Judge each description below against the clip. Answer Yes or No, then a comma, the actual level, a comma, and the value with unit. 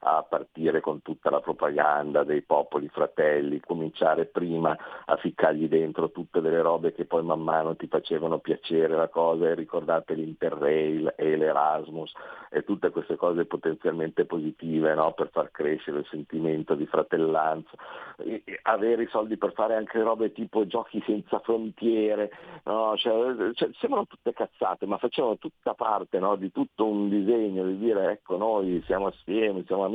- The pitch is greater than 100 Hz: No, very low, 95 Hz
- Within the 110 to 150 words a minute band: No, average, 160 wpm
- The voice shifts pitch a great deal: Yes, wide, 6.0 semitones